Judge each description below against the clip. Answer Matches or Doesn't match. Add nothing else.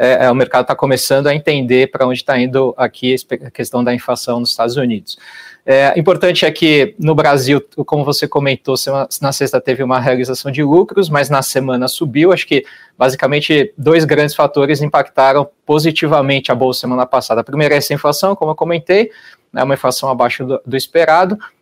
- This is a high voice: Doesn't match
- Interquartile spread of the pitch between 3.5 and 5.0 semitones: Doesn't match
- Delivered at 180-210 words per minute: Matches